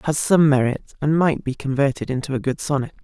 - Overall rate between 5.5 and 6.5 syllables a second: Yes, 6.0 syllables/s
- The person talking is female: Yes, female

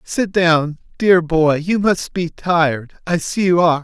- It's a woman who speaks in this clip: No, male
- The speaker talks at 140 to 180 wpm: No, average, 190 wpm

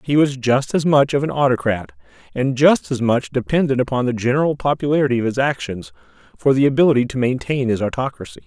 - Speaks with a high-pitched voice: No, low, 125 Hz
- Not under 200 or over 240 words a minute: No, average, 190 wpm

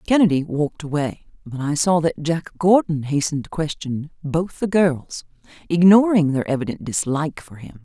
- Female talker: Yes, female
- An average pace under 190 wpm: Yes, average, 160 wpm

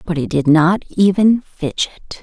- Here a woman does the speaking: Yes, female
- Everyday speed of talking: Yes, average, 160 wpm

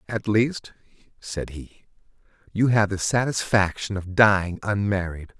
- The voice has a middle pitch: No, low, 100 Hz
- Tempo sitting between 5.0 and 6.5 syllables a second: No, 4.2 syllables/s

